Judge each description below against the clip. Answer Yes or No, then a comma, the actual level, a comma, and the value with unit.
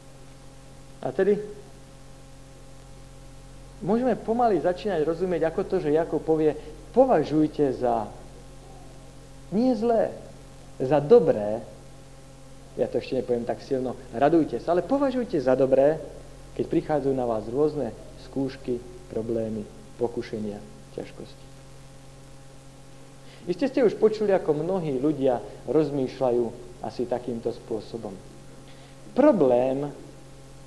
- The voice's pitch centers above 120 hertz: Yes, low, 135 Hz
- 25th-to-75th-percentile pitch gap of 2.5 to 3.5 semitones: Yes, average, 3.2 semitones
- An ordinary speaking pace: No, slow, 100 wpm